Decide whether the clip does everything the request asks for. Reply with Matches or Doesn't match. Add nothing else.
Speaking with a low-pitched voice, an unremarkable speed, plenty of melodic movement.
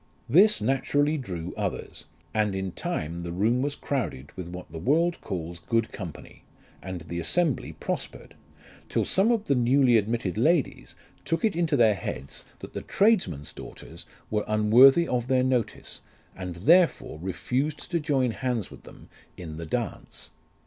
Matches